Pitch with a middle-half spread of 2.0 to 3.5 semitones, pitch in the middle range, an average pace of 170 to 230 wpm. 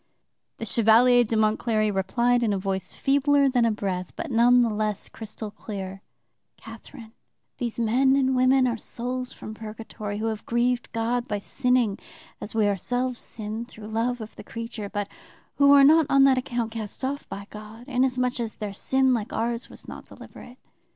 No: average, 2.8 semitones; high, 230 Hz; average, 180 wpm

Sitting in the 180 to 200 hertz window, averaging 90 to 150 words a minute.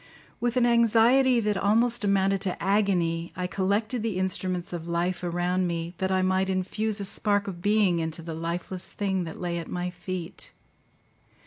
No: high, 190 Hz; average, 175 wpm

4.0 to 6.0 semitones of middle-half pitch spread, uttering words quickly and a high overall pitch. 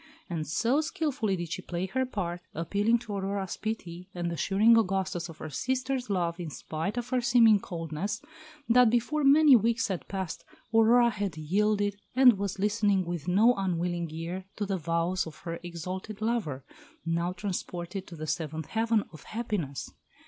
No: average, 4.8 semitones; average, 165 wpm; high, 195 Hz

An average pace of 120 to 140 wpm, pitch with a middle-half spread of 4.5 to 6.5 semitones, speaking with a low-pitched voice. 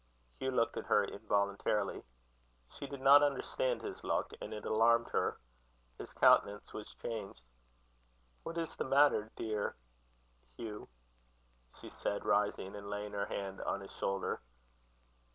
Yes: slow, 135 wpm; average, 5.0 semitones; low, 110 Hz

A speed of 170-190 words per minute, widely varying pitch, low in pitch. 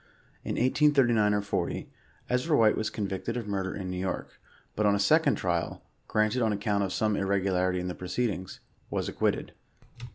No: average, 175 wpm; average, 3.1 semitones; low, 105 Hz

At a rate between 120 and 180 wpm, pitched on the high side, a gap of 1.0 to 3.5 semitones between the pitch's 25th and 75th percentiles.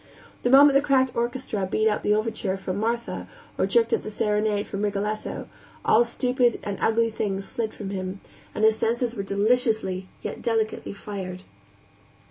Yes: average, 165 wpm; high, 215 Hz; average, 3.0 semitones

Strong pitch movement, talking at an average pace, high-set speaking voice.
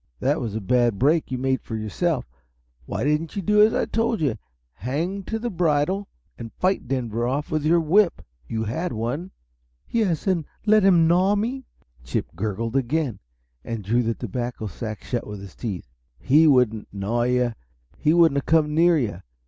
No: wide, 6.8 semitones; average, 180 wpm; medium, 140 Hz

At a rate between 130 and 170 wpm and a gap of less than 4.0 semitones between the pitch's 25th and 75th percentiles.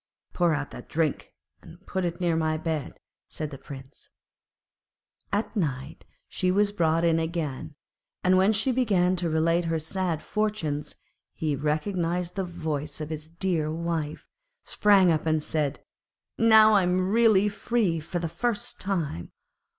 Yes: average, 150 wpm; average, 3.5 semitones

